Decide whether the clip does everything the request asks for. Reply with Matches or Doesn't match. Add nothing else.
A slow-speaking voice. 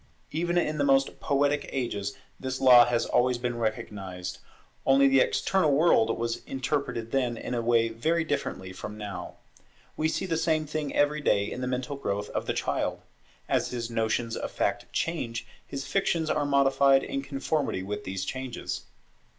Doesn't match